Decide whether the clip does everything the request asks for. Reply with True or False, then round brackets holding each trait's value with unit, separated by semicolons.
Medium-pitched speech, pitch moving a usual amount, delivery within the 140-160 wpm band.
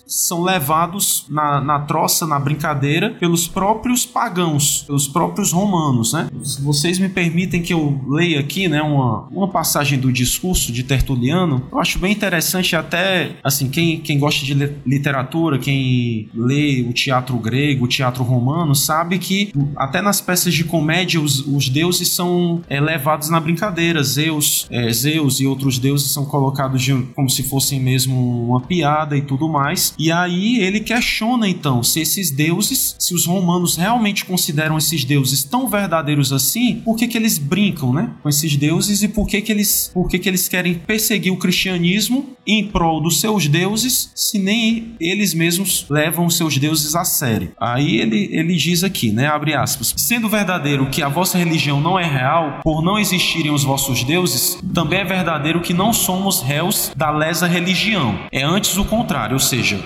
False (165 Hz; 4.8 semitones; 175 wpm)